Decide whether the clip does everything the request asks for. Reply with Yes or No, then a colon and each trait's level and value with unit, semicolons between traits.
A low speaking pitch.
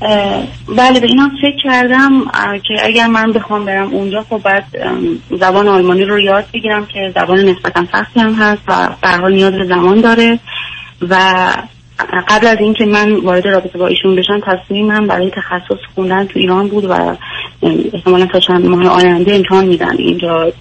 No: high, 195 Hz